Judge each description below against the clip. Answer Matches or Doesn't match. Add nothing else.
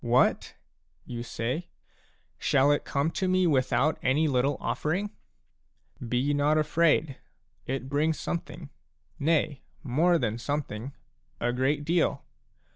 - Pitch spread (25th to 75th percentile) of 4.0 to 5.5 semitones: Doesn't match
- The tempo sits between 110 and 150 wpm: Matches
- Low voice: Doesn't match